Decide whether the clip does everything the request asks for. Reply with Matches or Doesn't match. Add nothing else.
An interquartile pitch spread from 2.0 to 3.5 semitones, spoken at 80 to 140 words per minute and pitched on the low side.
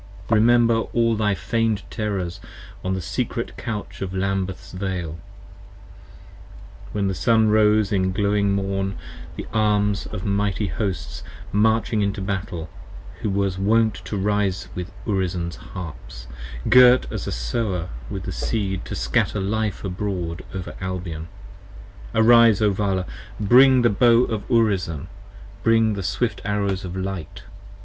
Matches